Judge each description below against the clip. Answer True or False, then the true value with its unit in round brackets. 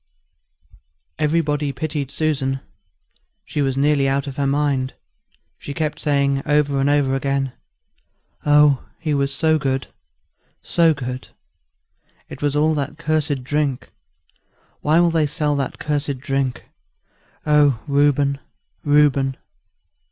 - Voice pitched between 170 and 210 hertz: False (145 Hz)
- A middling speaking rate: False (120 wpm)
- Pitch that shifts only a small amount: True (1.6 semitones)